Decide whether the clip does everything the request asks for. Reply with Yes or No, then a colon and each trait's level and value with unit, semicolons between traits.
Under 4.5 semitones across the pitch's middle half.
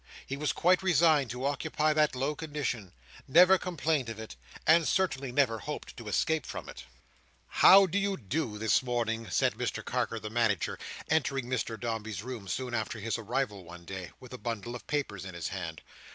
No: average, 5.3 semitones